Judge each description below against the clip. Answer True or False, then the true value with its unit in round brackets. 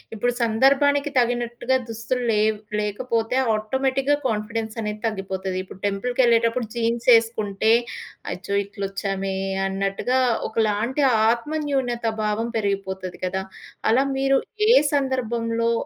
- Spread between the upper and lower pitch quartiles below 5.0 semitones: True (3.3 semitones)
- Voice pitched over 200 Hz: True (230 Hz)